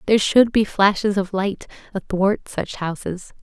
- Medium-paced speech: Yes, average, 160 wpm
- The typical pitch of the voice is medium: No, high, 200 Hz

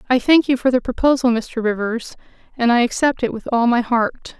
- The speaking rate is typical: No, fast, 220 wpm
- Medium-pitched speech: No, high, 245 Hz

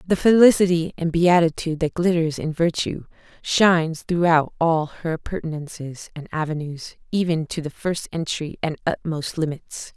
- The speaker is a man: No, female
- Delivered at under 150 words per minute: Yes, average, 140 wpm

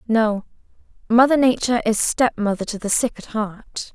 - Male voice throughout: No, female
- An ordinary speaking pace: Yes, average, 150 wpm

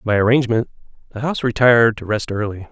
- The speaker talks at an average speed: Yes, average, 175 wpm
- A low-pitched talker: Yes, low, 115 Hz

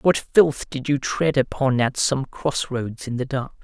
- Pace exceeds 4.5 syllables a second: No, 4.0 syllables/s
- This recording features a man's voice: Yes, male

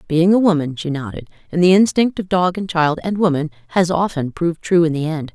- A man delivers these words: No, female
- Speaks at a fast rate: Yes, fast, 235 wpm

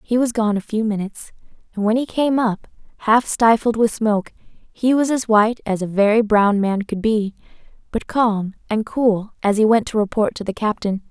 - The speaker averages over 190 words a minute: Yes, fast, 205 wpm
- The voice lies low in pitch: No, high, 220 Hz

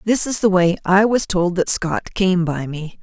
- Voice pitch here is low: No, medium, 185 Hz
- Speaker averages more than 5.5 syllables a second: No, 4.4 syllables/s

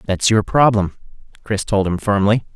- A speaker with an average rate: Yes, average, 165 wpm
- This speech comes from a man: Yes, male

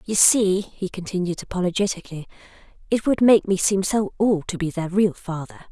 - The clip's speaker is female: Yes, female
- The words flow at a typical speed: Yes, average, 180 wpm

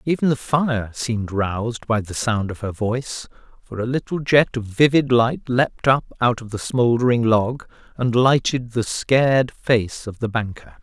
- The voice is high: No, low, 120 Hz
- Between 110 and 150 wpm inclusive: No, average, 185 wpm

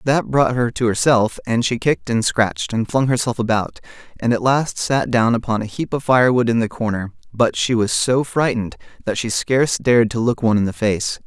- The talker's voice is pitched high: No, low, 115 Hz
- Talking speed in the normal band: No, fast, 225 wpm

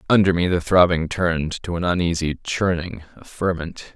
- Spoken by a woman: No, male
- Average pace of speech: Yes, average, 165 wpm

